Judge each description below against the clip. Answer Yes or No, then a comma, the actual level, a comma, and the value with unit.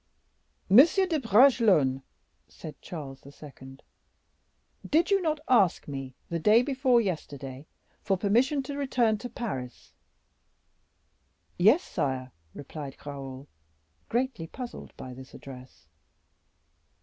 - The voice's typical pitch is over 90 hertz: Yes, high, 190 Hz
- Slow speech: Yes, slow, 105 wpm